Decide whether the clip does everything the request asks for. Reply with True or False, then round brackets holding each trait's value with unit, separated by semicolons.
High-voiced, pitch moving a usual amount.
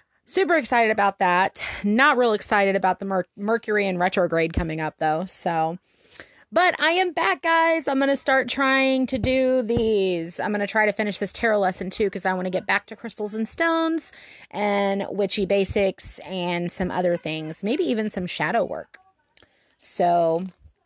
False (205 Hz; 5.8 semitones)